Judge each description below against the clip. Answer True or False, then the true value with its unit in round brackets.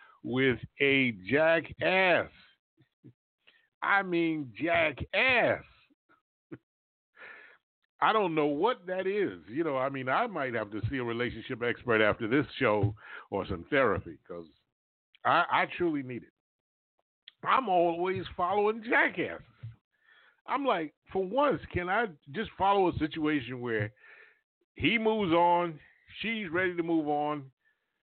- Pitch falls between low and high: True (165 Hz)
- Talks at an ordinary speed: False (125 wpm)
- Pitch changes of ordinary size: False (8.0 semitones)